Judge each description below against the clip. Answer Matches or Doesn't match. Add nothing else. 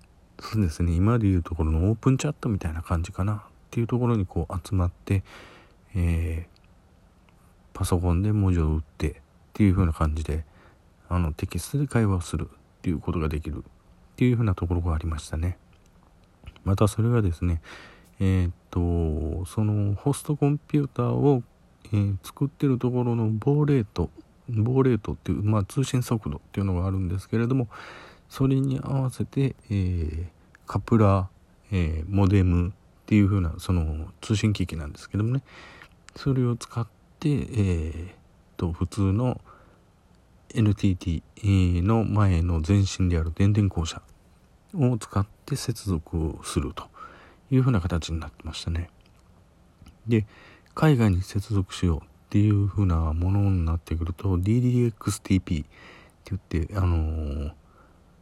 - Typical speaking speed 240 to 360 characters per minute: Matches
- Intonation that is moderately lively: Matches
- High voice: Doesn't match